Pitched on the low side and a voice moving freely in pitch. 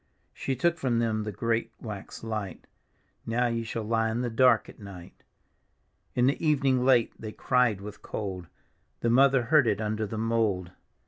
No: low, 115 Hz; average, 2.7 semitones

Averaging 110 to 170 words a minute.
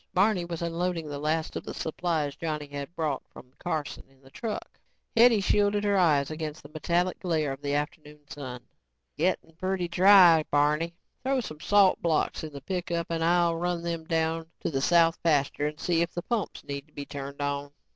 No: average, 195 wpm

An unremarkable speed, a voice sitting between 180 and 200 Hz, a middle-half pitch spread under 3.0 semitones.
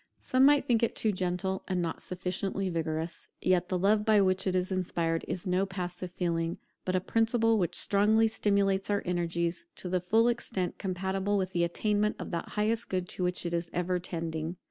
Yes: average, 195 wpm; medium, 185 Hz; narrow, 2.6 semitones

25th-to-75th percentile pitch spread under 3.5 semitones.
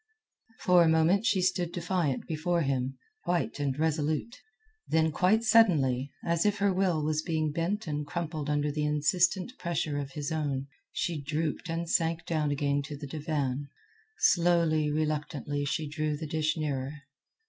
Yes: average, 2.8 semitones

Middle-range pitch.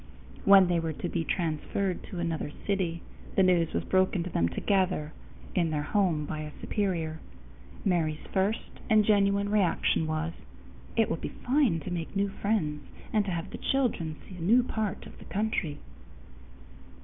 Yes: medium, 180 Hz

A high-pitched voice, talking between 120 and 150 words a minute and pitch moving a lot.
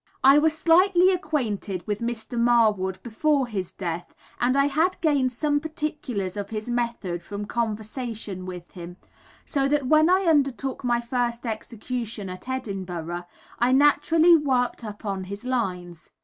Yes: high, 240 Hz; average, 145 wpm; wide, 6.1 semitones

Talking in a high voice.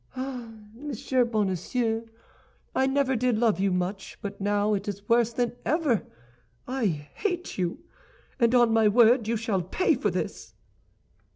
Yes: high, 230 Hz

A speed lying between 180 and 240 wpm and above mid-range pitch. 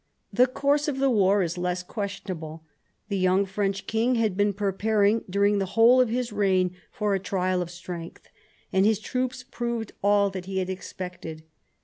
Yes: average, 185 wpm; high, 200 Hz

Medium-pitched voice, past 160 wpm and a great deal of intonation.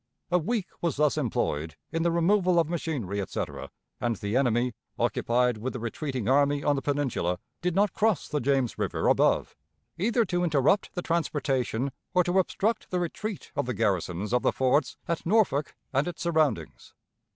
Yes: medium, 145 Hz; average, 175 wpm; wide, 6.1 semitones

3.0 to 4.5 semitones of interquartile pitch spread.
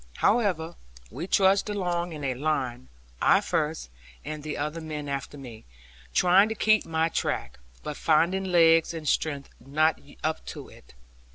Yes: average, 3.4 semitones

